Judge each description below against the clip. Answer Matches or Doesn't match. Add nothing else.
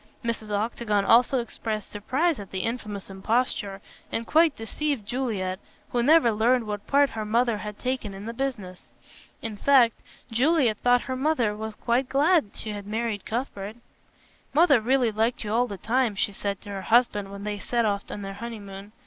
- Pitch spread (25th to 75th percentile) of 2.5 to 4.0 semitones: Matches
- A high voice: Matches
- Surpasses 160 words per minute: Matches